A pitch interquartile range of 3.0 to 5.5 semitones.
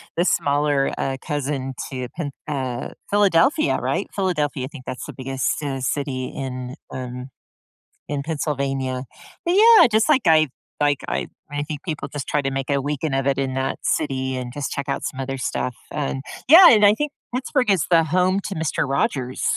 Yes: average, 3.8 semitones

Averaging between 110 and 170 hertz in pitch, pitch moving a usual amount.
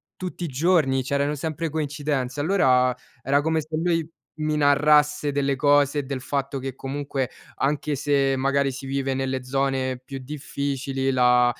No: medium, 140 Hz; narrow, 1.9 semitones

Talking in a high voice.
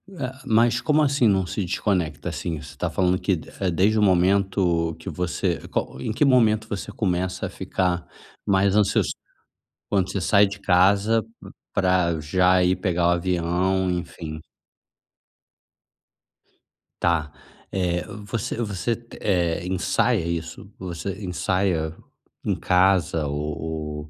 No: very low, 90 Hz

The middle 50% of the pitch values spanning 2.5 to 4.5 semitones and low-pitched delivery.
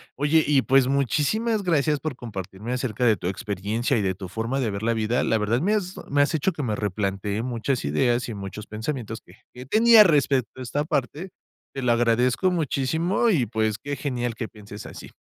No: average, 5.1 semitones; low, 125 Hz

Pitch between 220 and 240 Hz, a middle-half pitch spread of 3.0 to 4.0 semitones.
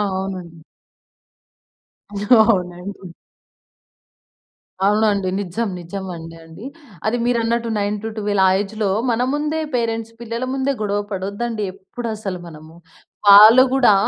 No: high, 210 Hz; average, 3.3 semitones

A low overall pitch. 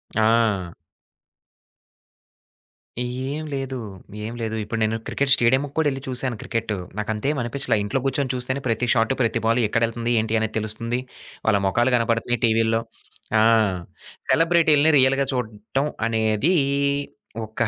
Yes: low, 115 Hz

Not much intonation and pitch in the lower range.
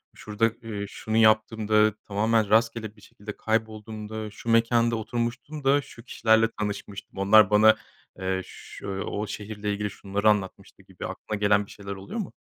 Yes: narrow, 1.6 semitones; low, 110 Hz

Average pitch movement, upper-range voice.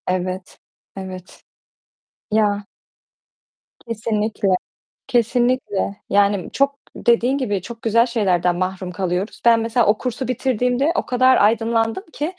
Yes: average, 3.9 semitones; high, 225 Hz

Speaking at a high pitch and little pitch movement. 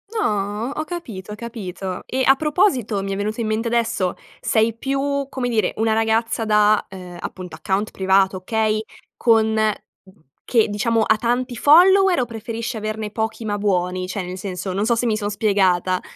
No: high, 220 Hz; average, 3.1 semitones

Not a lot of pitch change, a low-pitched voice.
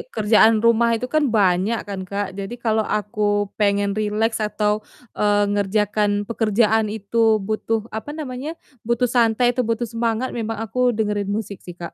No: narrow, 2.1 semitones; high, 220 Hz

